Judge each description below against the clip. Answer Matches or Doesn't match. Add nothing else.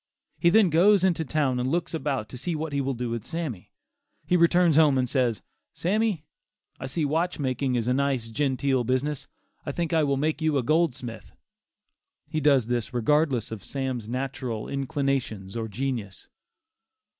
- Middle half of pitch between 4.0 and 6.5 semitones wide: Matches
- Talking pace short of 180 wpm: Matches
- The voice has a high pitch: Doesn't match